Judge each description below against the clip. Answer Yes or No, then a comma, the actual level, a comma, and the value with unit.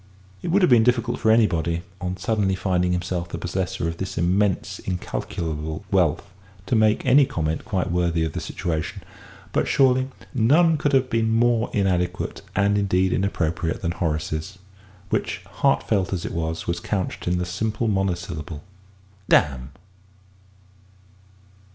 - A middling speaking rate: Yes, average, 145 wpm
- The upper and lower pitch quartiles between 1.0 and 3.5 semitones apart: No, average, 4.6 semitones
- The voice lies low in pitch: Yes, very low, 95 Hz